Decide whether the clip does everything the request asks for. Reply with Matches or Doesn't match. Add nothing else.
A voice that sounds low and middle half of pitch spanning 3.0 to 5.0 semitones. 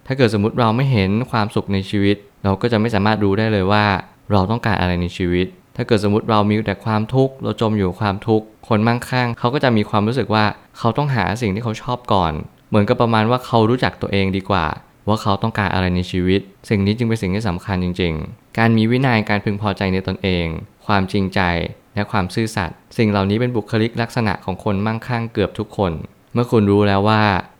Doesn't match